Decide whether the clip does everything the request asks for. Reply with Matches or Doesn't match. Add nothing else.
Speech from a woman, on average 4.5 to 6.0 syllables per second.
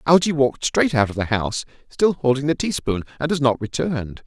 Doesn't match